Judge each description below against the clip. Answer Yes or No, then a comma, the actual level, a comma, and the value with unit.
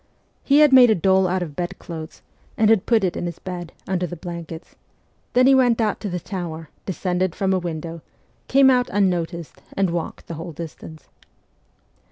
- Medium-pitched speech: Yes, medium, 180 Hz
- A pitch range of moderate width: Yes, average, 3.5 semitones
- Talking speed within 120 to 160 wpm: No, average, 180 wpm